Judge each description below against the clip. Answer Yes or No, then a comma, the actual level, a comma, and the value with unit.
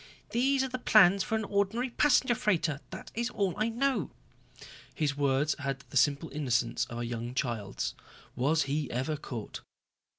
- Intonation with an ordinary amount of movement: No, wide, 8.8 semitones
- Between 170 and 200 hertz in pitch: No, medium, 155 Hz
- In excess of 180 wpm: No, average, 165 wpm